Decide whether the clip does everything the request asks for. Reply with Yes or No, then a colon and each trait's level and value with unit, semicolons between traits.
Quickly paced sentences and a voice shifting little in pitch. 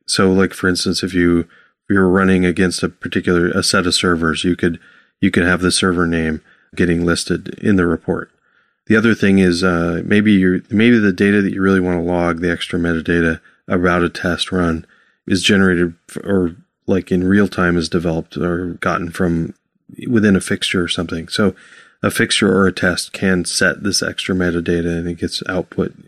No: average, 195 wpm; narrow, 1.8 semitones